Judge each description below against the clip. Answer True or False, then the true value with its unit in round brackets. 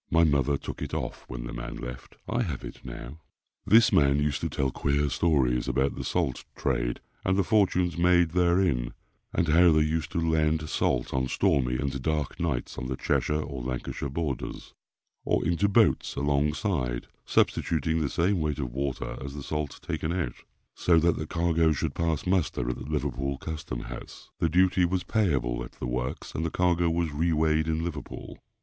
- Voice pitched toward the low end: True (75 Hz)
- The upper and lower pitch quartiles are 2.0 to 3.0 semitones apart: False (4.2 semitones)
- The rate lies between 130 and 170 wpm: False (185 wpm)